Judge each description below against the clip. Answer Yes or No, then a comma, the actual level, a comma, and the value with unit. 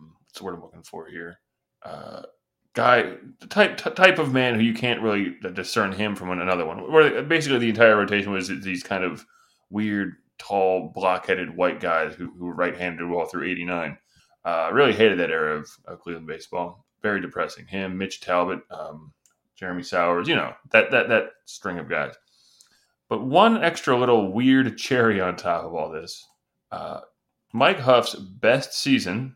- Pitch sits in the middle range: No, low, 105 Hz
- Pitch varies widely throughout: Yes, wide, 5.9 semitones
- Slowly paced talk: No, average, 175 wpm